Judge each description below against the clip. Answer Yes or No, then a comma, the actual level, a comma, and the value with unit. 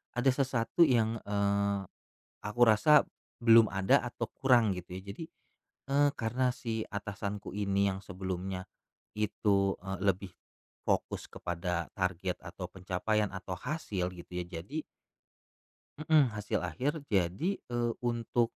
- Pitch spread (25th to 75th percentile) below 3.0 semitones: No, average, 4.1 semitones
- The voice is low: Yes, low, 105 Hz